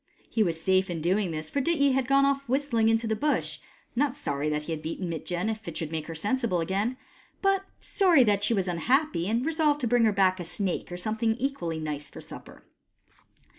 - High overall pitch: Yes, high, 215 Hz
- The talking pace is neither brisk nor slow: No, fast, 220 wpm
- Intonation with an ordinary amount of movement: No, wide, 7.8 semitones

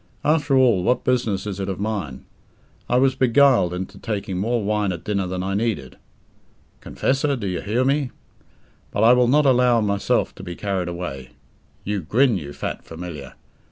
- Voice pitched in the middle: No, low, 105 Hz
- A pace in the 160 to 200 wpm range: Yes, average, 175 wpm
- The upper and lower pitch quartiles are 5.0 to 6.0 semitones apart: Yes, average, 5.3 semitones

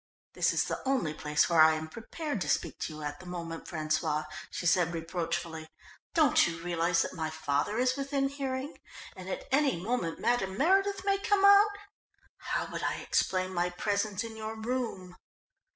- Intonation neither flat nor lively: No, wide, 8.1 semitones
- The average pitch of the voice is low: No, medium, 185 Hz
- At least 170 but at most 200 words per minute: Yes, average, 180 wpm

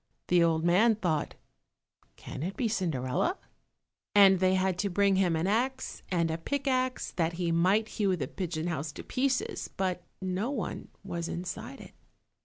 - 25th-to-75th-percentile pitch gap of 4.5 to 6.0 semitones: No, average, 4.0 semitones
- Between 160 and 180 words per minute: Yes, average, 165 wpm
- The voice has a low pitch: No, medium, 185 Hz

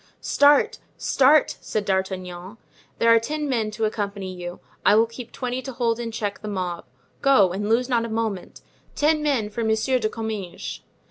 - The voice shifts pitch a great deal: No, average, 3.7 semitones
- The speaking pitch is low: No, high, 220 Hz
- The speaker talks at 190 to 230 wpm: No, average, 180 wpm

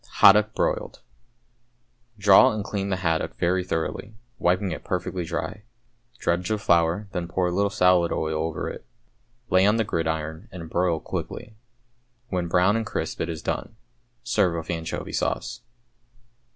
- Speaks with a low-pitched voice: Yes, very low, 90 Hz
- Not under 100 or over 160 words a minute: Yes, average, 150 wpm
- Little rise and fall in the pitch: No, average, 3.4 semitones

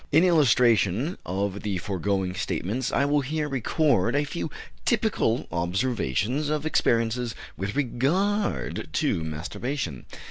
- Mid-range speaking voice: No, low, 120 Hz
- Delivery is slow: Yes, slow, 115 wpm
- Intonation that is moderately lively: No, wide, 7.1 semitones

